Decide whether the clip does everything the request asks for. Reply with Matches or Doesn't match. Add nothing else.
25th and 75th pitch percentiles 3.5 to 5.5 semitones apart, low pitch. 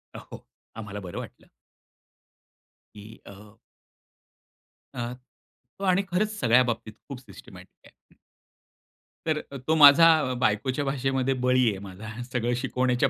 Matches